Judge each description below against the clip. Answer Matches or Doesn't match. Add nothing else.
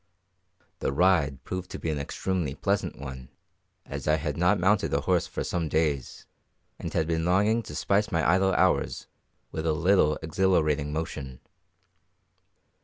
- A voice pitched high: Doesn't match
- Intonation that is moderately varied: Matches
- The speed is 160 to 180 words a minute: Doesn't match